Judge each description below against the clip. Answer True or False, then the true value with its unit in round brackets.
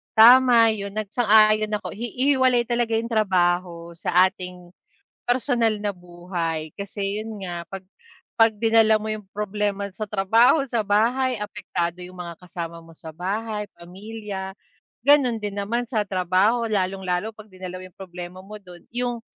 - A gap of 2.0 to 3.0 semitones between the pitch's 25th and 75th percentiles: False (3.7 semitones)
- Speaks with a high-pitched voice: True (205 Hz)